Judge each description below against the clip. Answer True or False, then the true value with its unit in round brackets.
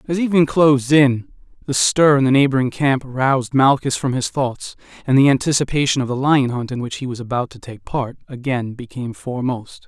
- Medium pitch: False (130 Hz)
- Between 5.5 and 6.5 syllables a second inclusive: True (5.7 syllables/s)